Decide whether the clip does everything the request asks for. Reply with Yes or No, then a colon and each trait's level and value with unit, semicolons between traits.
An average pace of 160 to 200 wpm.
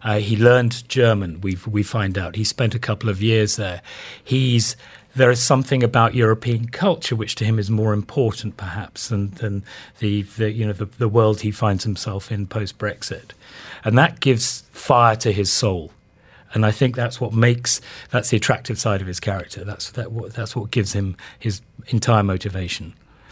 Yes: average, 190 wpm